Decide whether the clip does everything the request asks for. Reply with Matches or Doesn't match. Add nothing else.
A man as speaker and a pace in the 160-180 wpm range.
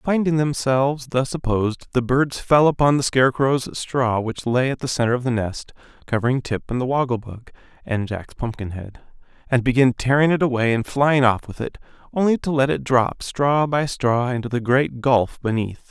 Doesn't match